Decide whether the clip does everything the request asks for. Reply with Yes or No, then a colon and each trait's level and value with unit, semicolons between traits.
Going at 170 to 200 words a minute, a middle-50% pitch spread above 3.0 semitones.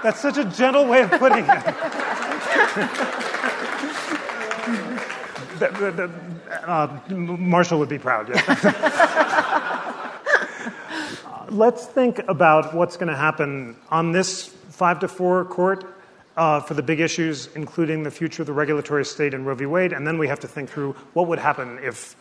No: average, 150 wpm; average, 4.1 semitones